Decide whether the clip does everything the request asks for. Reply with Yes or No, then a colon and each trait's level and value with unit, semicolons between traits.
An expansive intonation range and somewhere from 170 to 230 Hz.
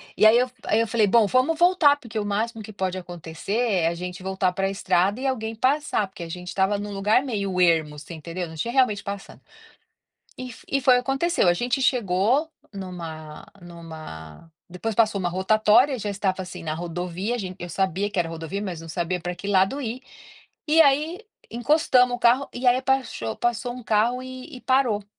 Yes: wide, 5.8 semitones; high, 205 Hz